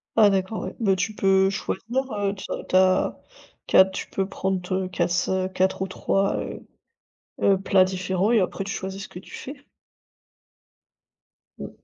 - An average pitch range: No, narrow, 0.9 semitones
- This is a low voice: No, high, 190 Hz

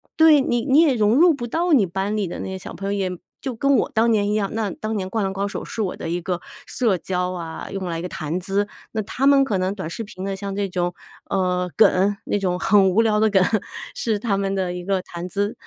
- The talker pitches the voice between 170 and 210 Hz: Yes, high, 200 Hz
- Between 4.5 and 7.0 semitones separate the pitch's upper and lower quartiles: No, average, 3.2 semitones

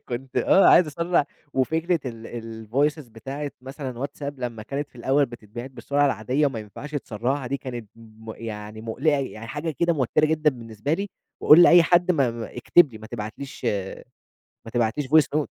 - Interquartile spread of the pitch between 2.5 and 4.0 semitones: No, average, 4.6 semitones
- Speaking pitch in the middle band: No, low, 130 Hz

